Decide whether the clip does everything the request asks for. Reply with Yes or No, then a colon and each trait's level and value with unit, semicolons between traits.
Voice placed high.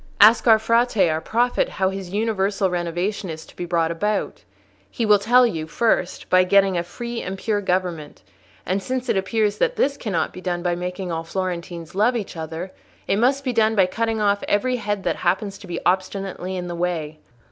Yes: high, 195 Hz